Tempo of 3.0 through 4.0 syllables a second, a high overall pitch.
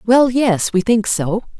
Yes: 3.8 syllables/s; high, 220 Hz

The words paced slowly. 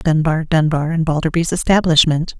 Yes: slow, 125 wpm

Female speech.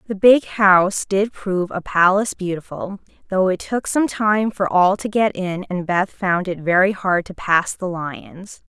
Yes: female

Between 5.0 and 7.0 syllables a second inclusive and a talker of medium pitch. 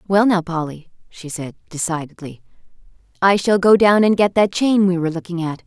Yes: 5.5 syllables/s; medium, 180 Hz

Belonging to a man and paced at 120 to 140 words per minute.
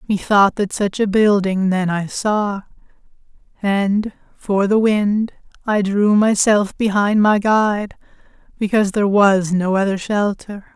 No: female; slow, 135 wpm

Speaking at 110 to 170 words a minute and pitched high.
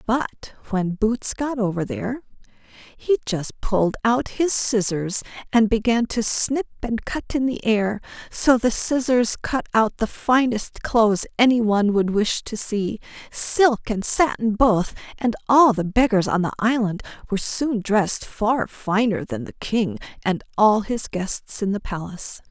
Yes: average, 165 wpm; high, 220 Hz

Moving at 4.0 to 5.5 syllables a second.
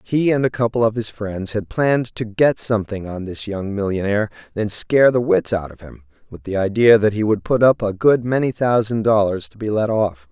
Yes: 5.4 syllables/s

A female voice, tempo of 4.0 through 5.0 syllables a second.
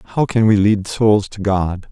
No: male; 4.5 syllables/s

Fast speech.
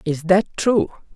No: average, 155 wpm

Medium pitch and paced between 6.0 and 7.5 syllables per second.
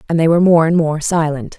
Yes: medium, 160 Hz; 6.4 syllables/s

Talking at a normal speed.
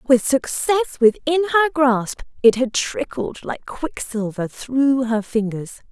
No: slow, 130 wpm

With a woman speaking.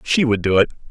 No: male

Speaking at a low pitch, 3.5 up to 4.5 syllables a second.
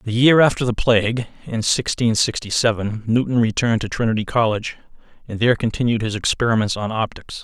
No: low, 115 Hz; 5.9 syllables/s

